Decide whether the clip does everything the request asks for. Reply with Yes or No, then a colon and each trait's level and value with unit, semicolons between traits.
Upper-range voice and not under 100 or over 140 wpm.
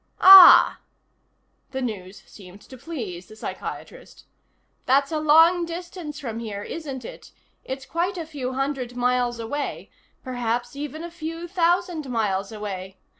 Yes: very high, 265 Hz; slow, 135 wpm